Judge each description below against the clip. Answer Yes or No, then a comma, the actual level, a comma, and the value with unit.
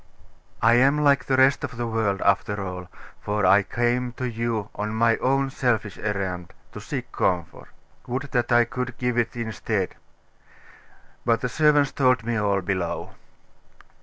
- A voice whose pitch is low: Yes, low, 115 Hz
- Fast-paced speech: No, average, 160 wpm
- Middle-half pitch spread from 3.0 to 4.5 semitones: Yes, average, 3.6 semitones